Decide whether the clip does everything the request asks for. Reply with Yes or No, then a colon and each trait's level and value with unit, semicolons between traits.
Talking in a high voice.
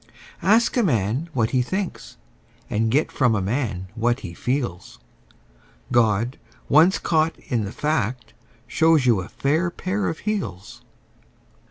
No: low, 125 Hz